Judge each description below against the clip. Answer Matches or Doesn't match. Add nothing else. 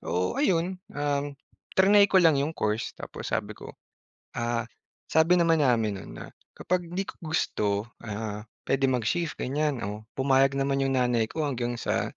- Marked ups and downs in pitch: Matches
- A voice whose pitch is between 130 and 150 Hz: Matches